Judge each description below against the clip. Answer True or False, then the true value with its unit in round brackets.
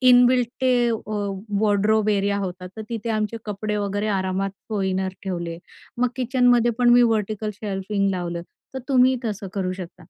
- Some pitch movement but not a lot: True (3.6 semitones)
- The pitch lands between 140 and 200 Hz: False (210 Hz)